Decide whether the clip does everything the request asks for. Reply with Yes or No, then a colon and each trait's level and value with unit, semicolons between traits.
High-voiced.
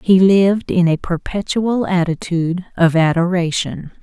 No: medium, 180 Hz